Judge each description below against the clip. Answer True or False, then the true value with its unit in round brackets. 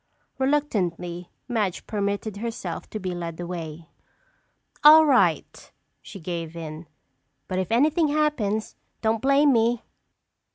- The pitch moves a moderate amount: False (7.2 semitones)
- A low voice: False (210 Hz)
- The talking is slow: True (115 wpm)